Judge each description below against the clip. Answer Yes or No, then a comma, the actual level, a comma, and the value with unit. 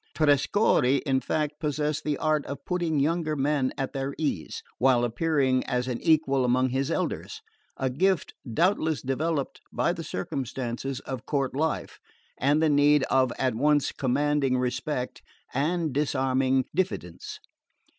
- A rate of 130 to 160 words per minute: Yes, average, 140 wpm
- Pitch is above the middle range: No, medium, 140 Hz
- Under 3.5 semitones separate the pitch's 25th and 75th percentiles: Yes, average, 2.8 semitones